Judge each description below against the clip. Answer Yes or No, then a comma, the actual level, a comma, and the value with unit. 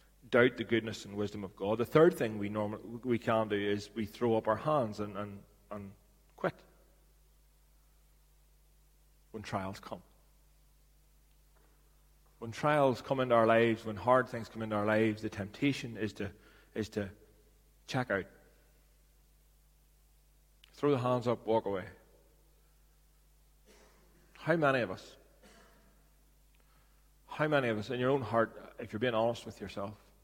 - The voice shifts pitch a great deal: No, narrow, 2.6 semitones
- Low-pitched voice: Yes, low, 110 Hz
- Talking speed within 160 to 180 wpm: No, average, 145 wpm